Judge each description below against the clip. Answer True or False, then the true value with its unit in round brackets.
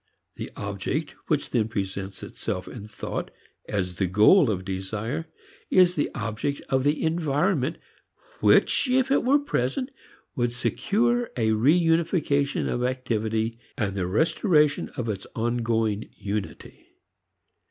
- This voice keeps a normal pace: False (130 wpm)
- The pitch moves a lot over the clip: True (7.1 semitones)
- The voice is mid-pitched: False (120 Hz)